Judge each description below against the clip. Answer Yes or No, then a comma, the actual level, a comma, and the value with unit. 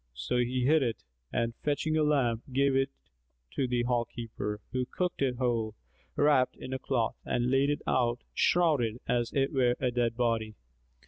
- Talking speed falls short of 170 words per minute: No, average, 180 wpm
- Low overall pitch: Yes, low, 125 Hz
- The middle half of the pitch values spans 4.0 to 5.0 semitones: No, narrow, 2.5 semitones